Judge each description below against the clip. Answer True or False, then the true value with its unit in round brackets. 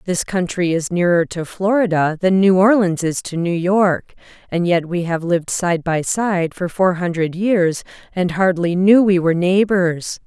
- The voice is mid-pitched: True (180 Hz)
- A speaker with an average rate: True (180 wpm)